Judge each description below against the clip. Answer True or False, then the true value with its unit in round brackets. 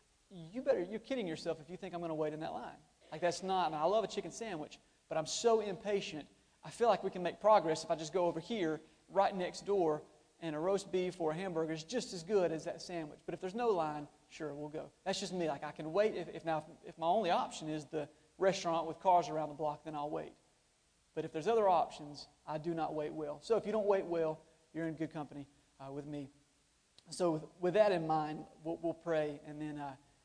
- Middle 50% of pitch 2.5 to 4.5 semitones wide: True (3.4 semitones)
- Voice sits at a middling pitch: True (160 Hz)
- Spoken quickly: True (255 wpm)